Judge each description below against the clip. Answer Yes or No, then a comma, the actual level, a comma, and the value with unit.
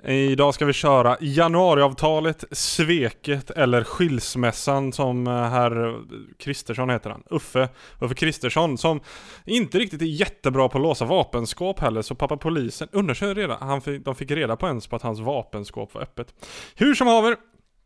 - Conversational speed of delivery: Yes, average, 150 wpm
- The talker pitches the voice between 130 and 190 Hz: Yes, medium, 140 Hz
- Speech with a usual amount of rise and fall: Yes, average, 4.7 semitones